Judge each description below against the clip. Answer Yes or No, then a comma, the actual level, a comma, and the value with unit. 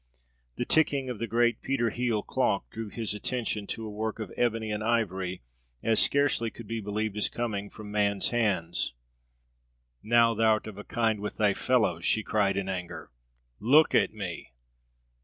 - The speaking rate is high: No, average, 170 wpm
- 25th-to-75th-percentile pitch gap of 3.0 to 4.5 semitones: No, narrow, 2.5 semitones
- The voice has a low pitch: Yes, low, 110 Hz